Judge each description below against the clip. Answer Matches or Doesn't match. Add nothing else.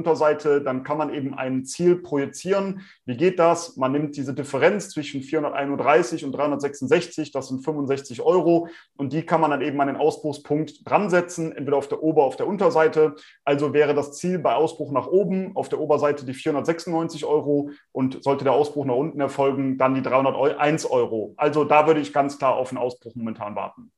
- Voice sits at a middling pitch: Matches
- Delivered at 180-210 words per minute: Matches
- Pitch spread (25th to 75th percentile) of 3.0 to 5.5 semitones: Doesn't match